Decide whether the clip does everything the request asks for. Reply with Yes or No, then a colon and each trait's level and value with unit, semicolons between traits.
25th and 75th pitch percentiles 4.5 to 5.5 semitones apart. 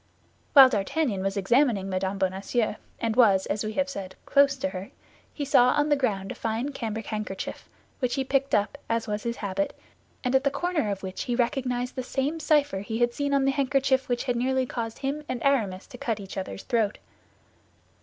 Yes: average, 5.0 semitones